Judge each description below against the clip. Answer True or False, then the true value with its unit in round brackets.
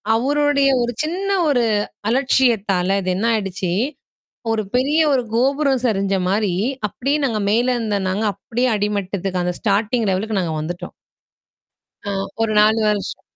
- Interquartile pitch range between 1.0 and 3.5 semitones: False (4.5 semitones)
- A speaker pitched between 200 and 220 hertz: True (215 Hz)